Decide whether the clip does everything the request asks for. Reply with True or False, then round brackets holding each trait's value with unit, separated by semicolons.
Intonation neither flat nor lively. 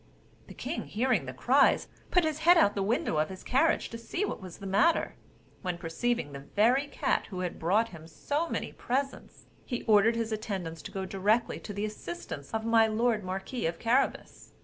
True (4.6 semitones)